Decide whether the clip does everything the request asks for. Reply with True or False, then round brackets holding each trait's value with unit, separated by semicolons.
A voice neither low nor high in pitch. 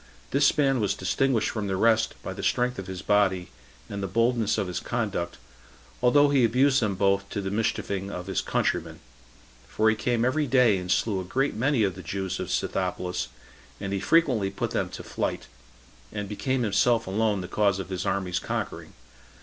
False (105 Hz)